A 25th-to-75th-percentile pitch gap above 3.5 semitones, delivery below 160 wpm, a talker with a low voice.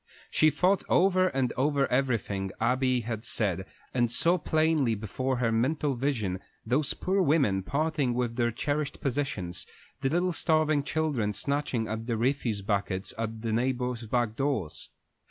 Yes: average, 4.5 semitones; average, 150 wpm; low, 125 Hz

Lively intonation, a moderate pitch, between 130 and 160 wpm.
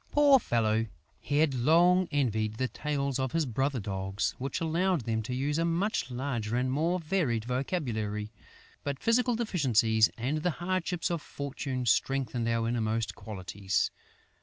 No: wide, 6.4 semitones; low, 130 Hz; average, 150 wpm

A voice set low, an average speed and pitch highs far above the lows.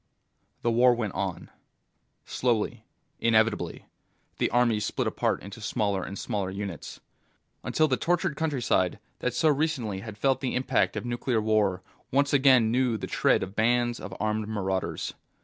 No: low, 115 Hz; average, 150 wpm; average, 3.8 semitones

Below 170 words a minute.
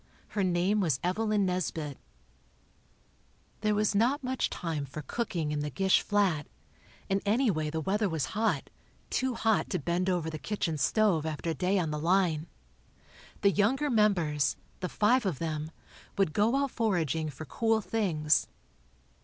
Yes: average, 155 wpm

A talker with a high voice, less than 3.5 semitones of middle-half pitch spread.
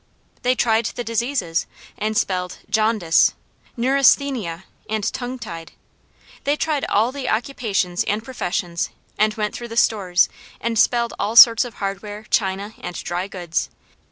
No: high, 215 Hz; average, 4.0 semitones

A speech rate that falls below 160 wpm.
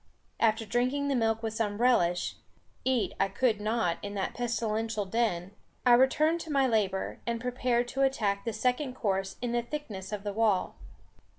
No: average, 175 wpm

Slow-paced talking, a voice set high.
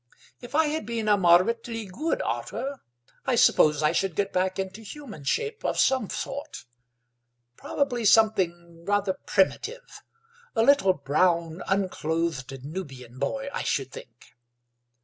Yes: slow, 130 wpm; high, 195 Hz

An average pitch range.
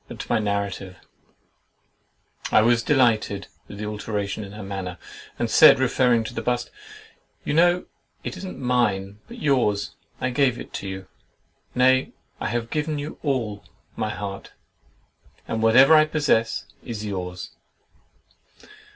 Yes: average, 4.3 semitones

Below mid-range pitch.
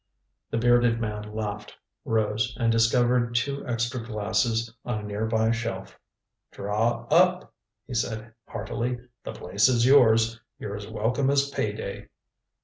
Yes: low, 115 Hz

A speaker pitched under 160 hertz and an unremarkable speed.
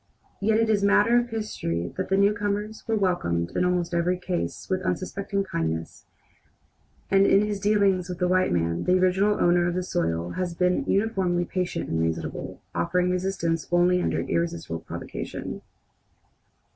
No: medium, 180 Hz; average, 160 wpm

